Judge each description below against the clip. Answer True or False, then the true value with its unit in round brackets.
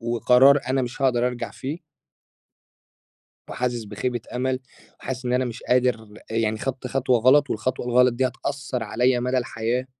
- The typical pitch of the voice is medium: False (125 Hz)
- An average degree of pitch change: False (1.5 semitones)